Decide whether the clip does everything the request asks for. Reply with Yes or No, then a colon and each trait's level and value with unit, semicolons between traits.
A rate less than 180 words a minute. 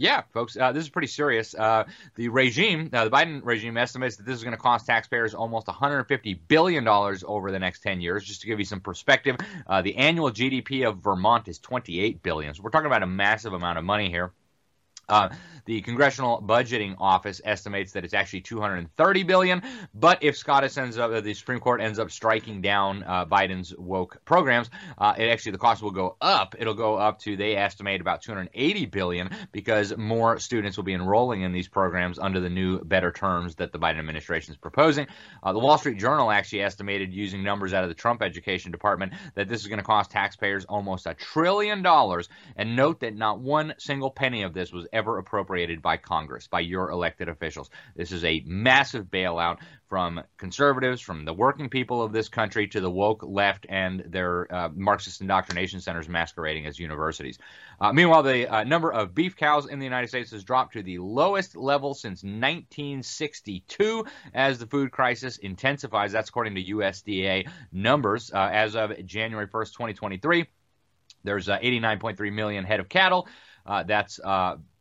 No: average, 190 wpm